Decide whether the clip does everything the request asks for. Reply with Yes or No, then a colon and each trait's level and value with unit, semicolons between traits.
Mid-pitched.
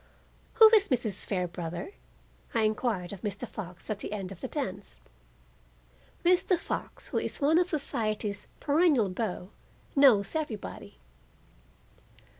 No: high, 215 Hz